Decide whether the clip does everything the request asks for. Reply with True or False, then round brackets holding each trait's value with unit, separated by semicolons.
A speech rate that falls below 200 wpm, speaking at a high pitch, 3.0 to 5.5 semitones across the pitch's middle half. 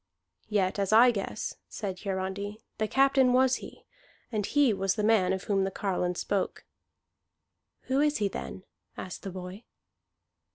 True (155 wpm; 200 Hz; 3.4 semitones)